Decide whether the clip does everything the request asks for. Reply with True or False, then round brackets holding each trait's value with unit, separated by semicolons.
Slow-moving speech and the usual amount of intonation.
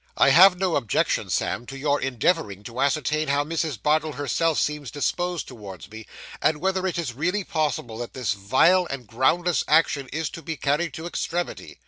False (180 wpm; 4.7 semitones)